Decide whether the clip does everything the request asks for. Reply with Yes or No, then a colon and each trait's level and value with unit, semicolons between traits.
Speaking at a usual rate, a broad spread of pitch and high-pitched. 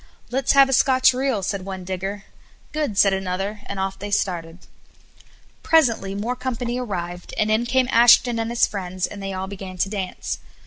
No: average, 180 wpm; average, 4.2 semitones; high, 205 Hz